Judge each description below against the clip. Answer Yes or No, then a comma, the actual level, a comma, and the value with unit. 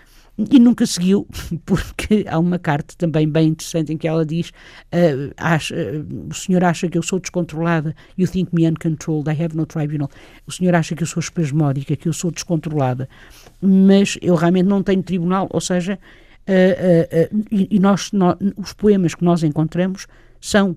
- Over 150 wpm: Yes, fast, 185 wpm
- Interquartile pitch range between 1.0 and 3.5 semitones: Yes, average, 2.8 semitones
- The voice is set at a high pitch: No, medium, 170 Hz